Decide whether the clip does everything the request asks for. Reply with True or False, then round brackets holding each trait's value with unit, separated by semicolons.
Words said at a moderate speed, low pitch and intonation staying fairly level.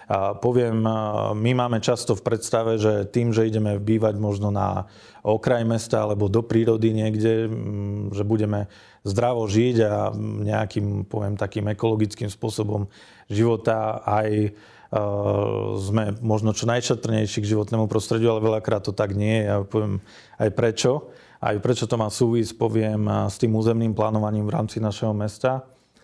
True (145 wpm; 110 Hz; 1.4 semitones)